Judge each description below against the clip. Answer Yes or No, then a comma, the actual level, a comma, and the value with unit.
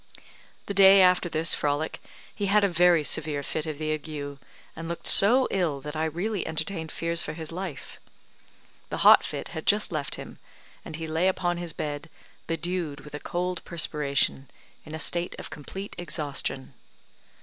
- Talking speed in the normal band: Yes, average, 170 wpm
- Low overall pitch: No, medium, 165 Hz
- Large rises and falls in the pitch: No, average, 2.9 semitones